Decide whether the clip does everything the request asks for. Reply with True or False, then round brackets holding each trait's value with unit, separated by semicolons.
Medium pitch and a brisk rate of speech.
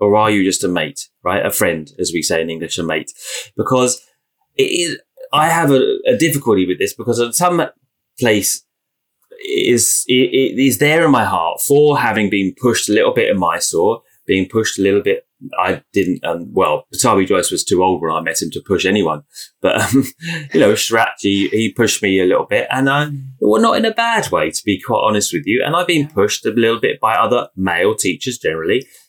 True (145 Hz; 225 wpm)